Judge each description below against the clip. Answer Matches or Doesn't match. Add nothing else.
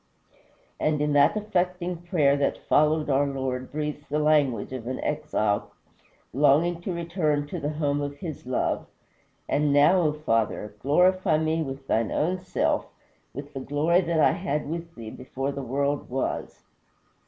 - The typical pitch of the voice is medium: Matches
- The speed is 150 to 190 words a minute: Matches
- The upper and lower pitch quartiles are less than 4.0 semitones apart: Matches